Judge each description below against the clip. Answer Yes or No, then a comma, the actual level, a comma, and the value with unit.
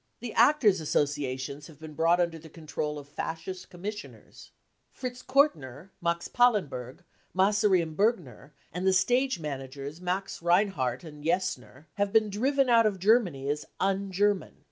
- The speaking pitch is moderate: Yes, medium, 180 Hz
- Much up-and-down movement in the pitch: Yes, wide, 5.7 semitones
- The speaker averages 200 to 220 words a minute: No, average, 155 wpm